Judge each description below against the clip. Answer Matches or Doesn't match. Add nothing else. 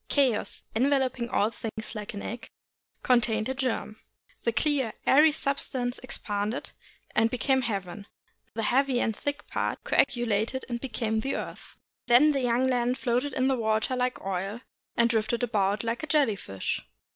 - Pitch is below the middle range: Doesn't match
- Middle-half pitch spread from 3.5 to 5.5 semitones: Doesn't match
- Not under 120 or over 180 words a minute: Matches